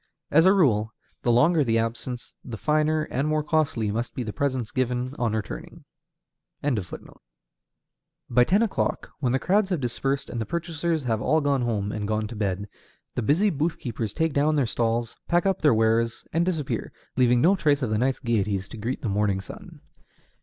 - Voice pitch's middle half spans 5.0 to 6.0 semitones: Yes, wide, 5.4 semitones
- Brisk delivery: No, average, 190 wpm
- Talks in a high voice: No, low, 125 Hz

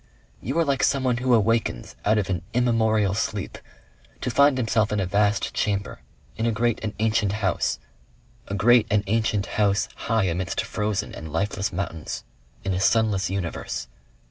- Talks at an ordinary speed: Yes, average, 165 wpm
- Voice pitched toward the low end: Yes, low, 105 Hz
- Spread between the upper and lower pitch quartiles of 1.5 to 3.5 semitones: Yes, average, 2.7 semitones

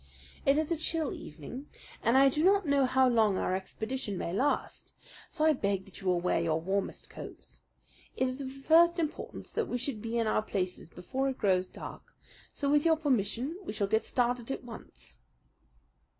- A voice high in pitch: Yes, very high, 250 Hz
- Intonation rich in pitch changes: Yes, wide, 6.3 semitones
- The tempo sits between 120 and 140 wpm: No, average, 195 wpm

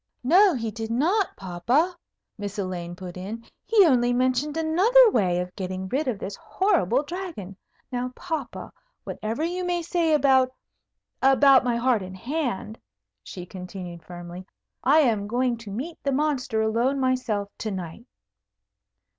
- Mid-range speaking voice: No, high, 245 Hz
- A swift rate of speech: No, average, 145 wpm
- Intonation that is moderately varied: No, wide, 7.4 semitones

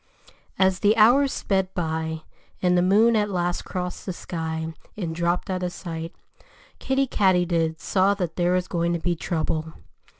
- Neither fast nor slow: Yes, average, 165 wpm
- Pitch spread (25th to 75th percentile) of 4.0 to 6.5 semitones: No, narrow, 2.6 semitones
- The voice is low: No, medium, 180 Hz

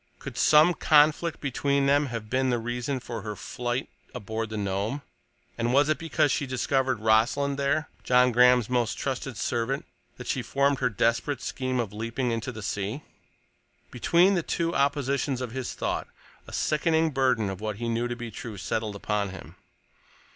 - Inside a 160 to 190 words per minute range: Yes, average, 170 wpm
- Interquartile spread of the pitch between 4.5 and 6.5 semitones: No, average, 3.7 semitones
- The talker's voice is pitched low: Yes, low, 125 Hz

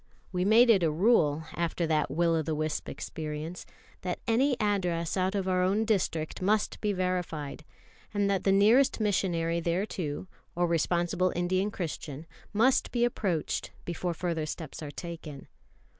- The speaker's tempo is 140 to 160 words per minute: Yes, average, 155 wpm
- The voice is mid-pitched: Yes, medium, 180 Hz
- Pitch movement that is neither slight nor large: Yes, average, 3.7 semitones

